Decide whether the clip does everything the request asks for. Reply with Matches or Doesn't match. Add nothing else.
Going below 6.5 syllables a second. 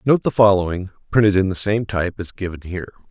Doesn't match